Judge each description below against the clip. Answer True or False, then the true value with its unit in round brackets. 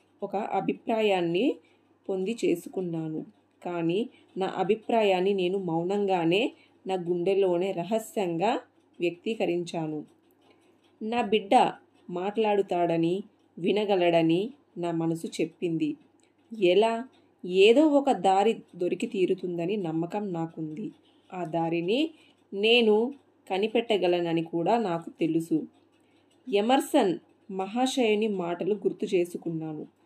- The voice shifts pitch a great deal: True (7.0 semitones)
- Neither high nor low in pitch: False (200 Hz)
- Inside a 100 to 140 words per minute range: False (80 wpm)